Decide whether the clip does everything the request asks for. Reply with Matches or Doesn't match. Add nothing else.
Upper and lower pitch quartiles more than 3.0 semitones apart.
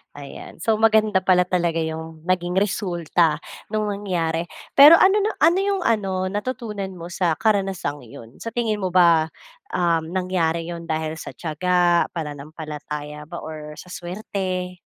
Matches